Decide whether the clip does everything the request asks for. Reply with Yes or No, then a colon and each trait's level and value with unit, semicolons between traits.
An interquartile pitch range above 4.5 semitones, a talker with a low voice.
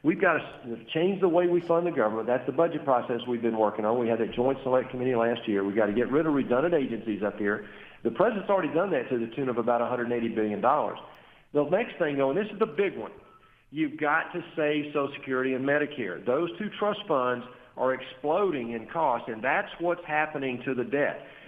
Yes: average, 5.1 semitones; low, 130 Hz